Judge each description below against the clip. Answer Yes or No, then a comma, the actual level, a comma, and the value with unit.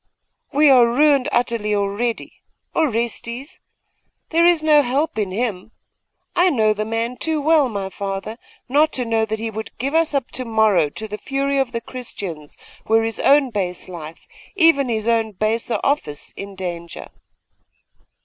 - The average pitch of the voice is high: Yes, high, 230 Hz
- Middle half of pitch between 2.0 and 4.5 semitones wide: No, average, 4.9 semitones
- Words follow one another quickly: No, average, 160 wpm